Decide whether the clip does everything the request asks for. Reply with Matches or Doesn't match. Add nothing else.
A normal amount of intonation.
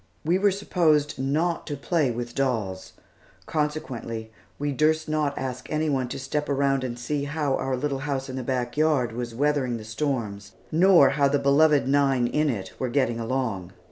Matches